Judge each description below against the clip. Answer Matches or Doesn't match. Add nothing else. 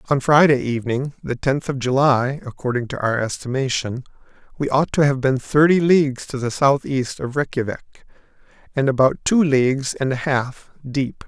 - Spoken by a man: Matches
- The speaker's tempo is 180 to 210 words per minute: Doesn't match